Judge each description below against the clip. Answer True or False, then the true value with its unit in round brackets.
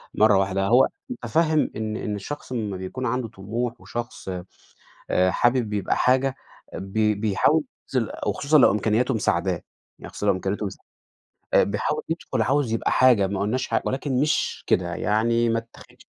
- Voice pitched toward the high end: False (115 Hz)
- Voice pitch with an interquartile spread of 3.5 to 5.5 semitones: True (3.9 semitones)